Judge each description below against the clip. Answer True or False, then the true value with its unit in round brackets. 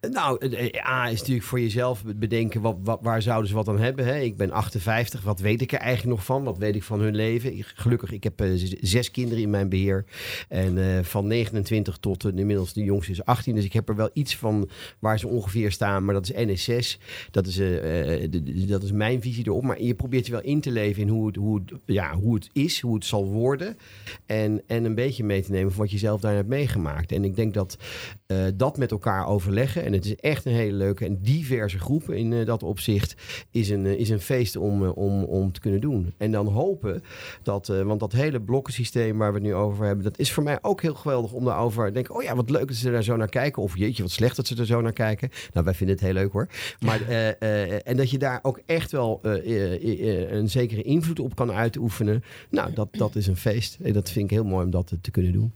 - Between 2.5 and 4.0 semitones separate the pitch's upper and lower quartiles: True (3.4 semitones)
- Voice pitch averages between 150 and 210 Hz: False (110 Hz)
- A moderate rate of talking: False (260 wpm)